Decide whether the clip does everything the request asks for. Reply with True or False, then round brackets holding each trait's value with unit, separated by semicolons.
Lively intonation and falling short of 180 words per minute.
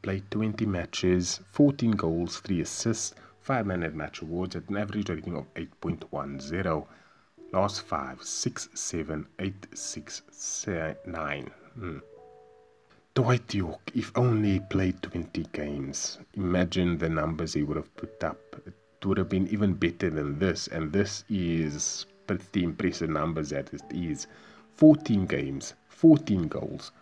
False (4.6 semitones; 140 wpm)